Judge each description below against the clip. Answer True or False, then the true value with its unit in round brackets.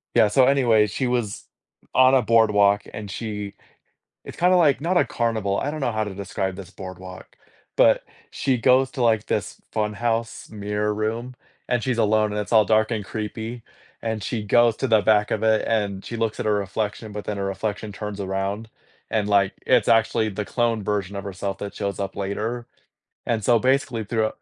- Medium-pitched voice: False (110 Hz)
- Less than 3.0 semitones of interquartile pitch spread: True (2.4 semitones)